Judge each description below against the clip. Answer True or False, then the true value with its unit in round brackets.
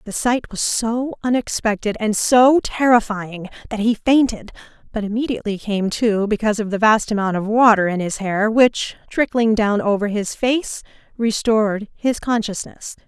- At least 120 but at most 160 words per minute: True (155 wpm)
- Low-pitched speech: False (220 Hz)